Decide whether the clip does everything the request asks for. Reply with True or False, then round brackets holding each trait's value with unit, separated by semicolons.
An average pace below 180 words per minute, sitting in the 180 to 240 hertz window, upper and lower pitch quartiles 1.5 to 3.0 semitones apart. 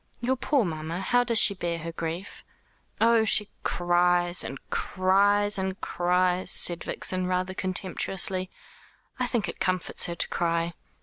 True (145 wpm; 185 Hz; 2.6 semitones)